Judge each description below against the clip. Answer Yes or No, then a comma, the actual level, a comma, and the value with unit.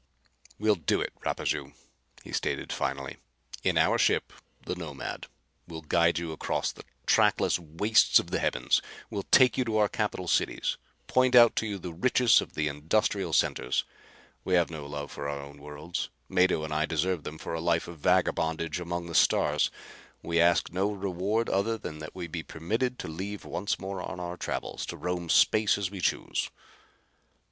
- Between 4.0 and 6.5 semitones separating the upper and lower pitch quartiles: Yes, average, 4.3 semitones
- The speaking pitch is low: Yes, very low, 85 Hz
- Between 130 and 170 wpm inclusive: No, average, 180 wpm